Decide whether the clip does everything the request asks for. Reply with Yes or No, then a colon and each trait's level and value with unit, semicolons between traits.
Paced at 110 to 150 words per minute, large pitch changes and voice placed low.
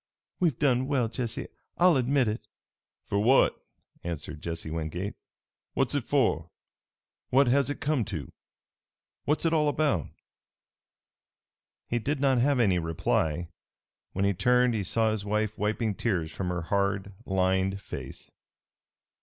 Yes: slow, 135 wpm; wide, 6.0 semitones; low, 110 Hz